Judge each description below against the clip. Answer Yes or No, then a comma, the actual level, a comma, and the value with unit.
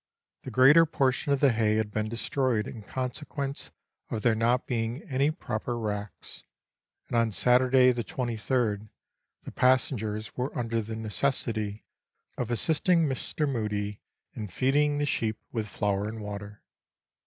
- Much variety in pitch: No, average, 3.6 semitones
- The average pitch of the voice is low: Yes, low, 120 Hz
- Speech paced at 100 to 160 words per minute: Yes, average, 145 wpm